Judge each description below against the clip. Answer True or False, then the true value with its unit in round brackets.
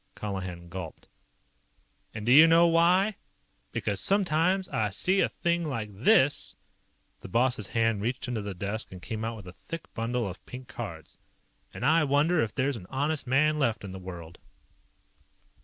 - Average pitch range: False (7.2 semitones)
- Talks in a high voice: False (120 Hz)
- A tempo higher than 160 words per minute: True (175 wpm)